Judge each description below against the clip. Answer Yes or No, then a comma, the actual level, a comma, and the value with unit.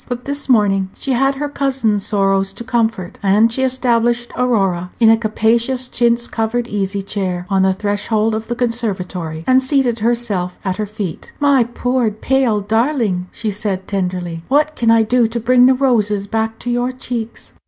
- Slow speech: No, average, 175 wpm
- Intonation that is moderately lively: Yes, average, 3.7 semitones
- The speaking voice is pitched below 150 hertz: No, high, 225 Hz